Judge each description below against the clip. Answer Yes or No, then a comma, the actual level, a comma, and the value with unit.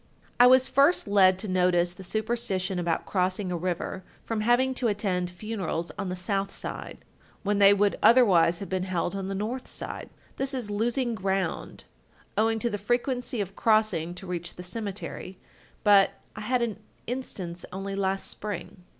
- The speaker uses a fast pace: No, average, 170 wpm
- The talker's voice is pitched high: Yes, high, 200 Hz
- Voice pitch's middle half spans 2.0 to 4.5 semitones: Yes, average, 3.6 semitones